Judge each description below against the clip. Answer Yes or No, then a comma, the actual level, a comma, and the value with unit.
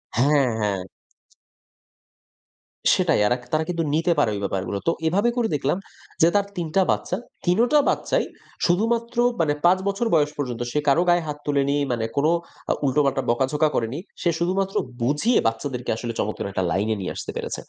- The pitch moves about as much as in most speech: No, wide, 6.3 semitones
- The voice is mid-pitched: Yes, medium, 150 Hz